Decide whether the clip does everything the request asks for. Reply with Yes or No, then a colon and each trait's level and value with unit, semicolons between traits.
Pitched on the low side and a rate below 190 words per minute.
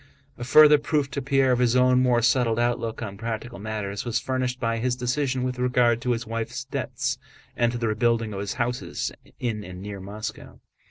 No: low, 120 Hz; average, 200 wpm